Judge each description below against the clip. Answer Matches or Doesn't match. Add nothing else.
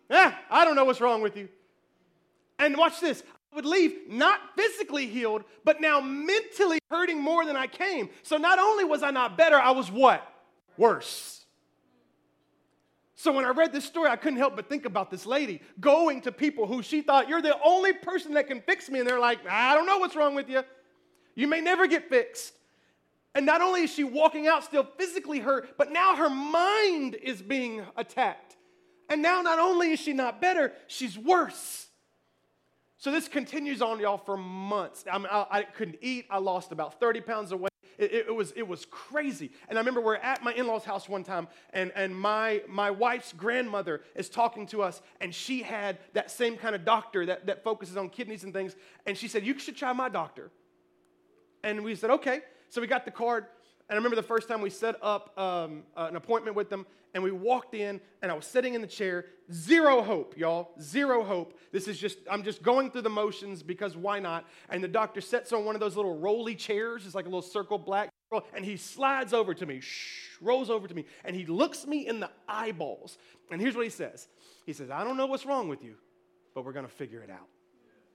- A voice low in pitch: Doesn't match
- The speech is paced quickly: Matches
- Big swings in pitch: Matches